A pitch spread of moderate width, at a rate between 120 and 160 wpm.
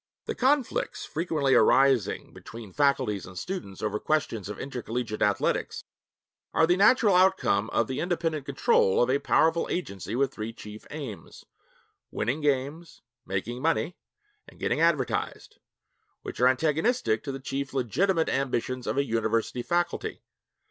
No: wide, 6.1 semitones; average, 140 wpm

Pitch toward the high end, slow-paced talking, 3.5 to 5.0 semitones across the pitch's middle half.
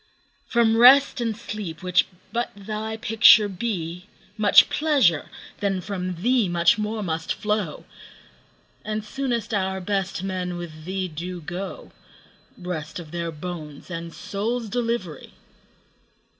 Yes: high, 195 Hz; slow, 130 wpm; average, 4.1 semitones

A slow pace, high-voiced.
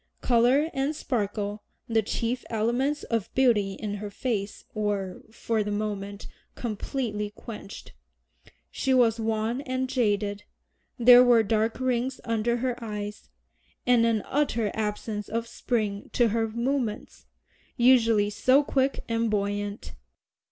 Yes: slow, 125 wpm; high, 225 Hz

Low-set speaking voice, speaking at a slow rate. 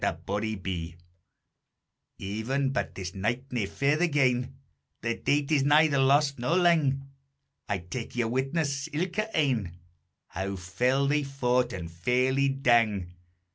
Yes: low, 130 Hz; slow, 125 wpm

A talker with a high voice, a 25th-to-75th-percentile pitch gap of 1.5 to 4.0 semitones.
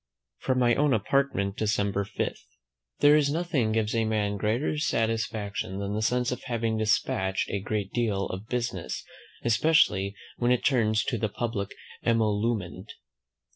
No: low, 110 Hz; average, 3.2 semitones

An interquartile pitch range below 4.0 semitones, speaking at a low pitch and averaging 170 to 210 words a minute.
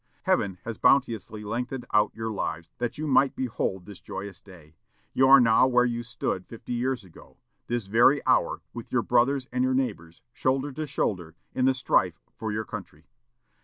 No: average, 4.5 semitones; low, 120 Hz; average, 180 wpm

